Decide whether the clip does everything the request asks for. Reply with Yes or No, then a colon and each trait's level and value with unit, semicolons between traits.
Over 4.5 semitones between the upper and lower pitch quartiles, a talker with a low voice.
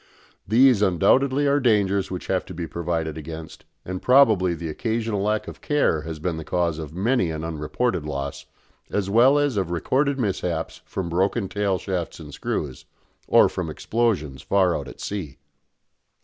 Yes: wide, 5.6 semitones; very low, 95 Hz